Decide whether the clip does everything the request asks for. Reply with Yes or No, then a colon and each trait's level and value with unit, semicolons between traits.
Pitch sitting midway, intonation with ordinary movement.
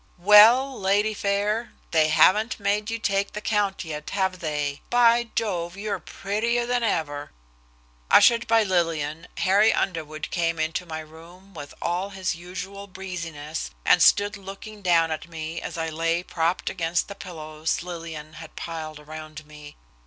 Yes: medium, 180 Hz; average, 4.2 semitones